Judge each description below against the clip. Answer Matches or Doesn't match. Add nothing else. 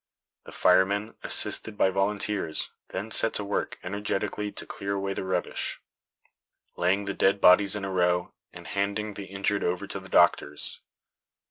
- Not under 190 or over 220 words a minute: Doesn't match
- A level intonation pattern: Matches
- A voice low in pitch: Matches